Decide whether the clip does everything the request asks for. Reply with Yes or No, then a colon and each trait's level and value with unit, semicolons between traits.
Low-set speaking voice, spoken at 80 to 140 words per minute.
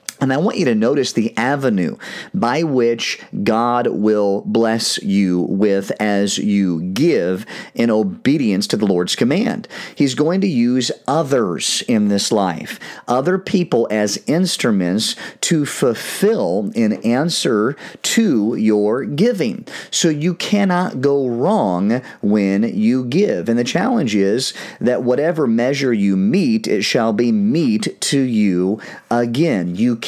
Yes: low, 125 Hz; slow, 135 wpm